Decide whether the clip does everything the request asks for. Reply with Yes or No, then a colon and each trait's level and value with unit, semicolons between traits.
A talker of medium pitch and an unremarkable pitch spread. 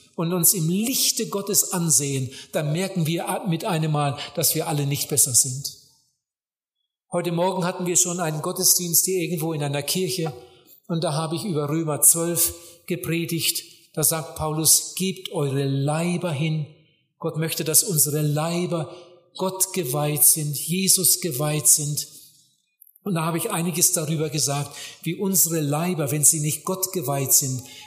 Yes: medium, 165 Hz; average, 3.1 semitones